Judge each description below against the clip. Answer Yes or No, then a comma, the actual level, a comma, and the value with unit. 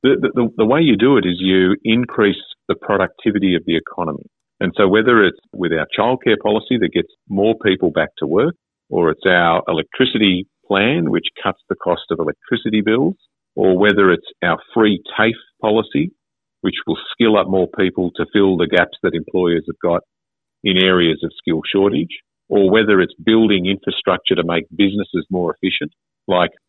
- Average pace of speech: Yes, average, 180 wpm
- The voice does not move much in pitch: Yes, narrow, 2.3 semitones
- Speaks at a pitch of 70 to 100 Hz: Yes, very low, 95 Hz